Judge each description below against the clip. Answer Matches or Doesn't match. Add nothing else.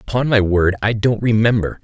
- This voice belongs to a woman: Doesn't match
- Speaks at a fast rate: Doesn't match